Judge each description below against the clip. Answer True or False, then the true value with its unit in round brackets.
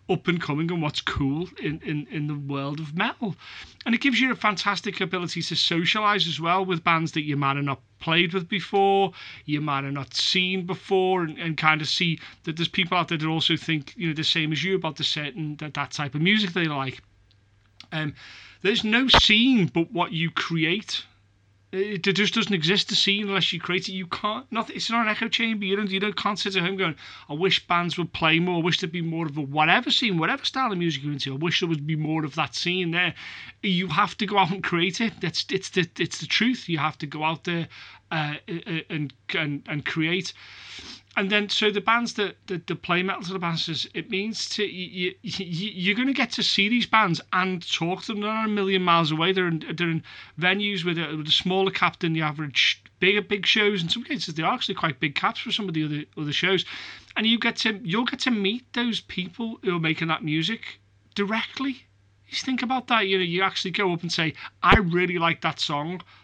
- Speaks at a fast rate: True (235 wpm)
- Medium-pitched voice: True (180 Hz)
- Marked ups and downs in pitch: False (4.3 semitones)